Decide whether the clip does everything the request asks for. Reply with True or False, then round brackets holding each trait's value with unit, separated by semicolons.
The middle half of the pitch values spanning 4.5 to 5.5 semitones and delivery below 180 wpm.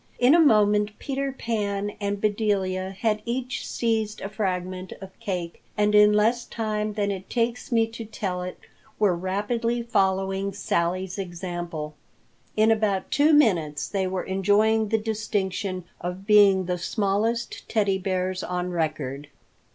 False (2.9 semitones; 145 wpm)